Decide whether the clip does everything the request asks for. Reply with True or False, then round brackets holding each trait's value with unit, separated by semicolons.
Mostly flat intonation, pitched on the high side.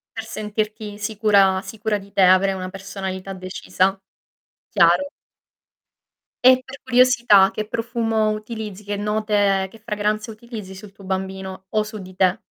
True (2.2 semitones; 210 Hz)